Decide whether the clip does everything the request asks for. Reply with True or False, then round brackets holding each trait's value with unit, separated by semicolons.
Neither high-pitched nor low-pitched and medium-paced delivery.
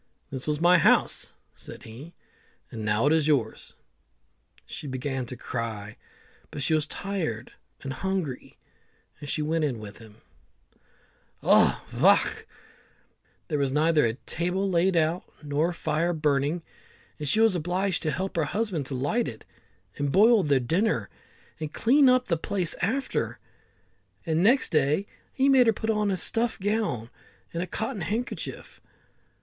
True (160 Hz; 150 wpm)